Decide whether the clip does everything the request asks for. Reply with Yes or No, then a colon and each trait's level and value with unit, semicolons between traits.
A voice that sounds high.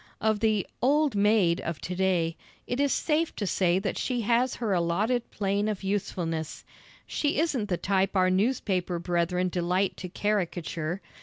Yes: high, 195 Hz